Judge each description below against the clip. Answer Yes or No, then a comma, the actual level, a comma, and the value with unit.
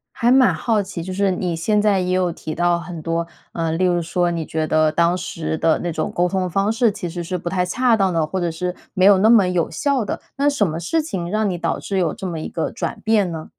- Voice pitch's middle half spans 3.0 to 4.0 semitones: Yes, average, 3.3 semitones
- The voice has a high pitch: No, medium, 180 Hz